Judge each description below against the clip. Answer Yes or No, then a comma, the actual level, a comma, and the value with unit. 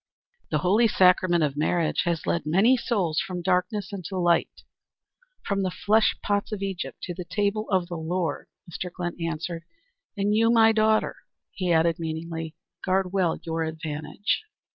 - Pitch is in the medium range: Yes, medium, 180 Hz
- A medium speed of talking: Yes, average, 160 wpm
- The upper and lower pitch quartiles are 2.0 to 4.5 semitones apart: Yes, average, 3.3 semitones